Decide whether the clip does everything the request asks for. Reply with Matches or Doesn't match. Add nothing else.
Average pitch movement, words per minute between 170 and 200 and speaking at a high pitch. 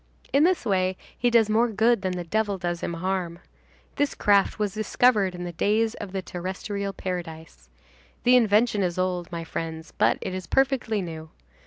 Matches